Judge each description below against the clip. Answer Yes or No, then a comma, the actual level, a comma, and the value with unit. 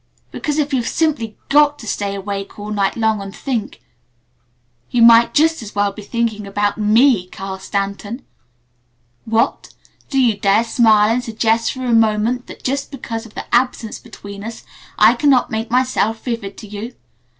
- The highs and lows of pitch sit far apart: No, average, 3.1 semitones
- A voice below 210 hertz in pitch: No, high, 225 Hz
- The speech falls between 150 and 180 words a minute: Yes, average, 170 wpm